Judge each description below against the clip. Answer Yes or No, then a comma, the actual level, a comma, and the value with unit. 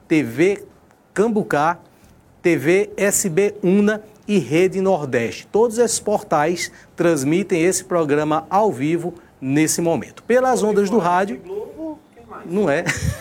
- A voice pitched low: No, high, 190 Hz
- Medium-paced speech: No, slow, 110 wpm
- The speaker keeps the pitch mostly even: No, average, 4.2 semitones